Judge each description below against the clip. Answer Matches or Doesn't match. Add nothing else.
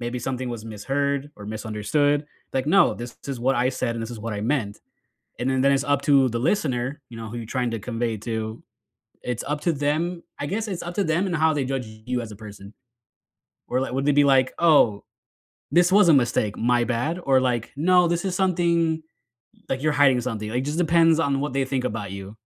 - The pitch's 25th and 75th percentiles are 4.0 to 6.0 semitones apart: Matches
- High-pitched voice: Doesn't match